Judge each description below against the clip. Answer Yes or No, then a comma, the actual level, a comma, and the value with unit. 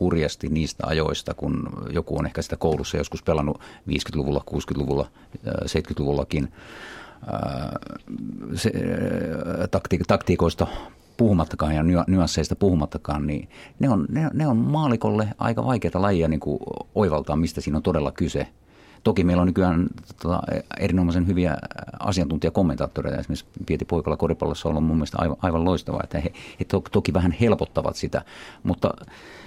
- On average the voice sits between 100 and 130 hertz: No, very low, 85 Hz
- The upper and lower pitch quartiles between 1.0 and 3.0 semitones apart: No, average, 3.5 semitones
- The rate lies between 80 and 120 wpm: No, average, 135 wpm